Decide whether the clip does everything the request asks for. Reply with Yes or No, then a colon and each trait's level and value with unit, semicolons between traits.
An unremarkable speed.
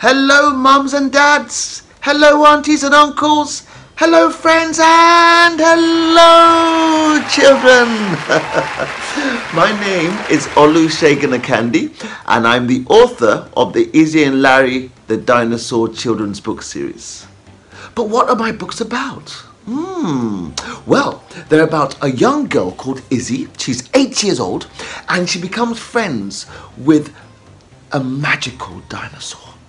No: slow, 120 wpm